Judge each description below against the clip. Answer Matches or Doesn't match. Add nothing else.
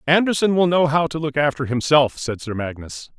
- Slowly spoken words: Doesn't match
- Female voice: Doesn't match